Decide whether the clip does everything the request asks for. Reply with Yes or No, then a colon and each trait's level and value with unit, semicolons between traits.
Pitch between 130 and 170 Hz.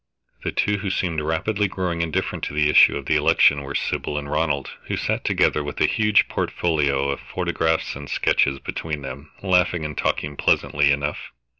No: very low, 75 Hz